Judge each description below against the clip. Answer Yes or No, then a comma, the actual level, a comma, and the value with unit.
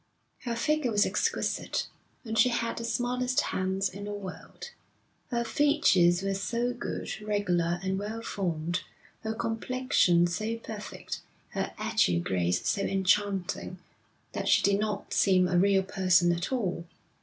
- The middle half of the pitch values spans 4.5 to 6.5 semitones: No, average, 4.0 semitones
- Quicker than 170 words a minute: No, average, 145 wpm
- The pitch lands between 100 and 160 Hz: No, high, 200 Hz